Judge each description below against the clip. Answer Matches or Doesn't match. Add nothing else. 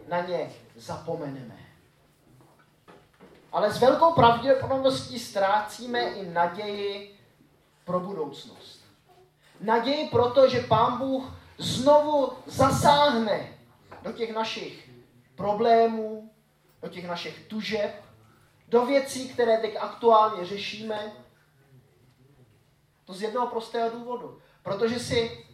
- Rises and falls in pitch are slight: Doesn't match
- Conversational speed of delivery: Doesn't match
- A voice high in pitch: Matches